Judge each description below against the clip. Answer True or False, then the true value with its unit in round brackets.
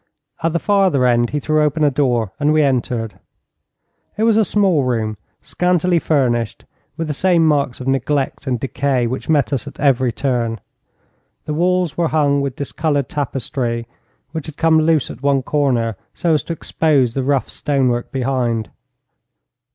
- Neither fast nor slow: True (165 wpm)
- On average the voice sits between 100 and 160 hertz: True (140 Hz)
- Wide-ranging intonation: False (4.0 semitones)